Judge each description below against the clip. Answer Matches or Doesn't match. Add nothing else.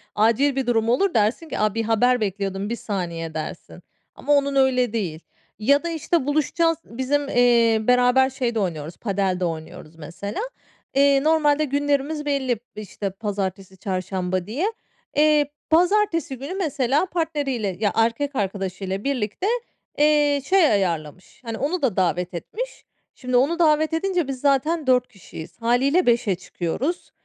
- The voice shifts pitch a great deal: Matches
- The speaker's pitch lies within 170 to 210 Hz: Doesn't match